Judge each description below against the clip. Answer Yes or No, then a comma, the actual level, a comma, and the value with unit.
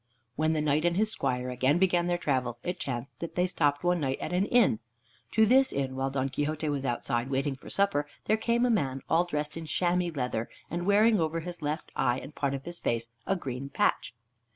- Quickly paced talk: Yes, fast, 225 wpm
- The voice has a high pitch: No, medium, 150 Hz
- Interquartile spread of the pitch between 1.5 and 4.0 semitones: No, average, 4.9 semitones